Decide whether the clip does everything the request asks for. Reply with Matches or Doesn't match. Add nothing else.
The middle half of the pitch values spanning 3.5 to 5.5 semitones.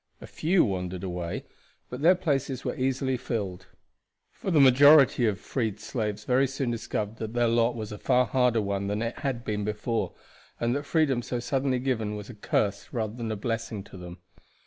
Matches